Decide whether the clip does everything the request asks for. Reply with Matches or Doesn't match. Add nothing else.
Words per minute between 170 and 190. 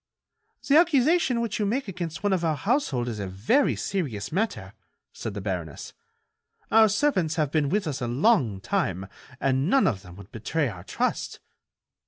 Matches